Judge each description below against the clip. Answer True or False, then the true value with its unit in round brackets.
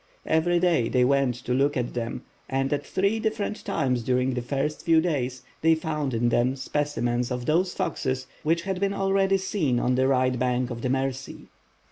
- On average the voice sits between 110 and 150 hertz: True (135 Hz)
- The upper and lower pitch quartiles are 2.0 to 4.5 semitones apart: False (4.9 semitones)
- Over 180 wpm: True (190 wpm)